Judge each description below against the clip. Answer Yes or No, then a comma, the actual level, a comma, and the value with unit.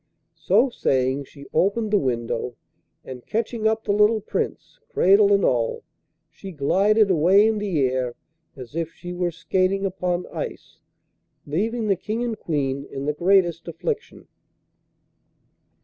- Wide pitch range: Yes, wide, 6.7 semitones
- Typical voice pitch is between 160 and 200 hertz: Yes, medium, 185 Hz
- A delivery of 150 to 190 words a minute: No, average, 140 wpm